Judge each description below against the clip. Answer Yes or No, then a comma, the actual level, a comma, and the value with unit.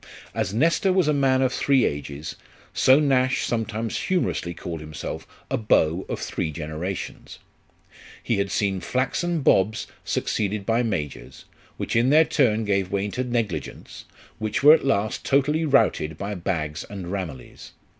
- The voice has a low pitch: Yes, low, 110 Hz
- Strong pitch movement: Yes, wide, 6.7 semitones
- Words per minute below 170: Yes, average, 150 wpm